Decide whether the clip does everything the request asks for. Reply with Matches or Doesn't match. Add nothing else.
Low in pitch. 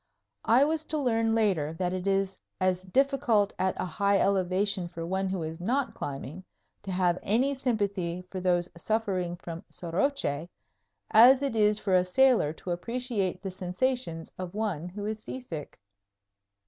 Doesn't match